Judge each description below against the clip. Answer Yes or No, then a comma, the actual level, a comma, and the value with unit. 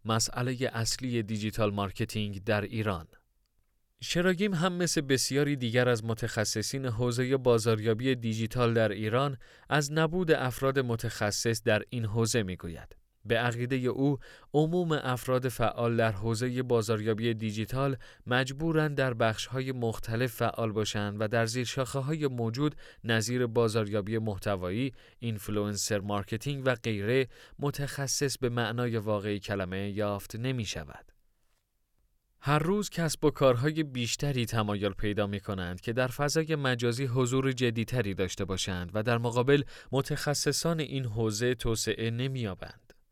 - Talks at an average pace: Yes, average, 125 wpm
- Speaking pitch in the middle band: No, low, 120 Hz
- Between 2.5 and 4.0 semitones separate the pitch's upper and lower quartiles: Yes, average, 3.4 semitones